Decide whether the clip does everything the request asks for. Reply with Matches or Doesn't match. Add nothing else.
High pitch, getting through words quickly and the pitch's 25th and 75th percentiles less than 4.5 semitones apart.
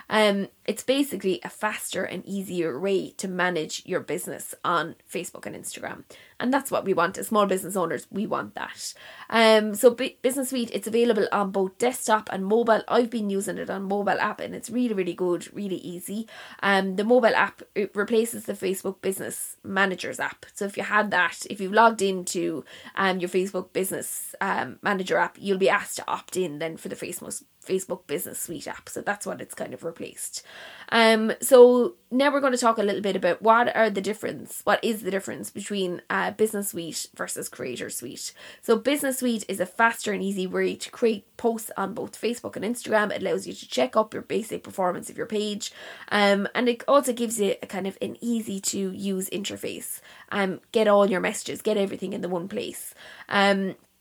Matches